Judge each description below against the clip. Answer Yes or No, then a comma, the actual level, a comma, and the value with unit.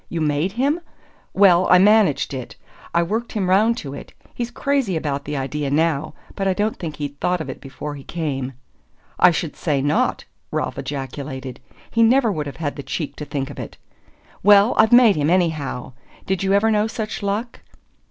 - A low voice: No, medium, 170 Hz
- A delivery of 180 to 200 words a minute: Yes, average, 190 wpm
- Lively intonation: Yes, wide, 6.4 semitones